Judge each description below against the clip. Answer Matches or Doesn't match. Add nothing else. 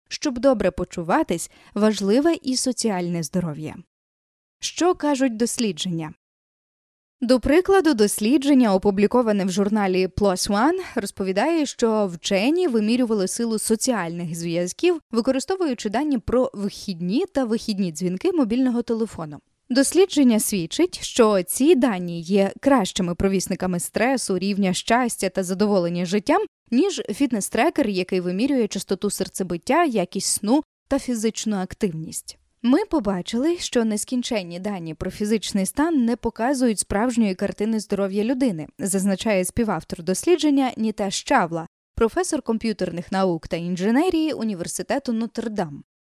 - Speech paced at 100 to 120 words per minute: Matches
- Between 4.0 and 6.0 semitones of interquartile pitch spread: Matches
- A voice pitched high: Matches